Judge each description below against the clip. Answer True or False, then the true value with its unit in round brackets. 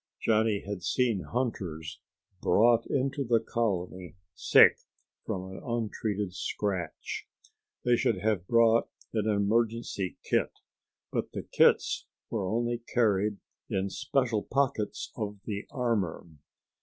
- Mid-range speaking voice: False (110 Hz)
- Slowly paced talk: True (115 wpm)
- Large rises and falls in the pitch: False (3.3 semitones)